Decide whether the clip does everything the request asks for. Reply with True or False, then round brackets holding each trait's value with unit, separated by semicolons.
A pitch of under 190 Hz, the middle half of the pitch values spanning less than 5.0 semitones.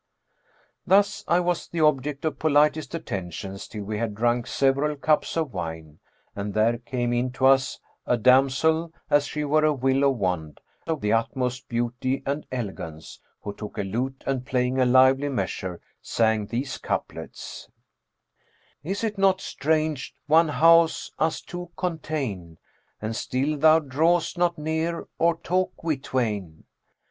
False (135 Hz; 5.4 semitones)